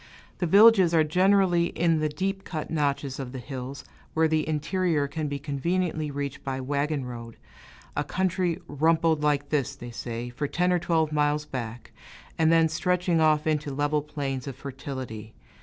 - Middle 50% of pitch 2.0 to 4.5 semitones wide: Yes, average, 3.1 semitones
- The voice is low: No, medium, 150 Hz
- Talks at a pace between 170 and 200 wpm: Yes, average, 175 wpm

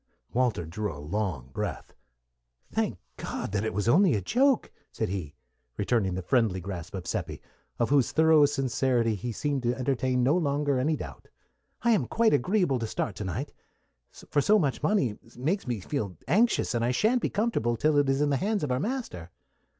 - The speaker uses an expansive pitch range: Yes, wide, 6.6 semitones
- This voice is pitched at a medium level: No, low, 130 Hz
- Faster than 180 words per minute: Yes, average, 190 wpm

